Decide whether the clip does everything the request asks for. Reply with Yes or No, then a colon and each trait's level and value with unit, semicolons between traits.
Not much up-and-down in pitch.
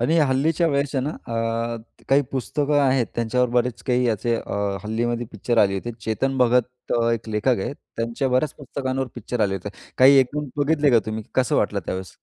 No: average, 3.1 semitones